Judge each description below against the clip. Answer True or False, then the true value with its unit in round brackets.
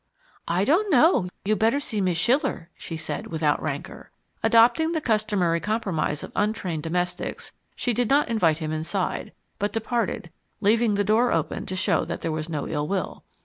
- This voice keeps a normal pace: True (175 wpm)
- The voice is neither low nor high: False (200 Hz)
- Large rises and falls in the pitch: True (5.7 semitones)